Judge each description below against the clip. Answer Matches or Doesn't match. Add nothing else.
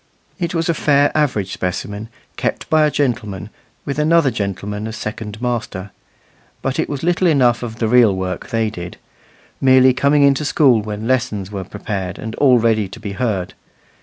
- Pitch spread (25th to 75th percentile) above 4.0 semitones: Matches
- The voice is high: Doesn't match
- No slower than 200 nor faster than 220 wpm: Doesn't match